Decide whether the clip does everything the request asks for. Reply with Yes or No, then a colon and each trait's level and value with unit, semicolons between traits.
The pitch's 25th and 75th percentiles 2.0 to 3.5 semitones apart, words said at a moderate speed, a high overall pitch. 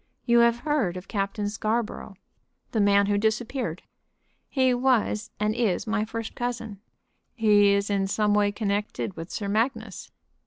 Yes: narrow, 2.6 semitones; average, 150 wpm; high, 215 Hz